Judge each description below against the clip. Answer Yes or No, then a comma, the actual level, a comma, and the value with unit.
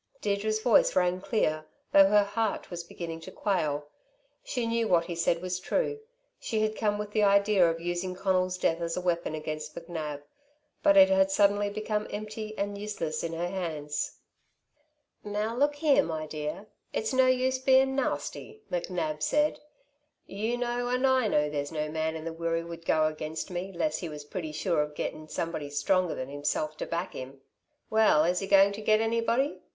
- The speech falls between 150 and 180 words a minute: No, average, 190 wpm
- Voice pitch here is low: No, medium, 185 Hz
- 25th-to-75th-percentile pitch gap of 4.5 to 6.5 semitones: Yes, average, 5.2 semitones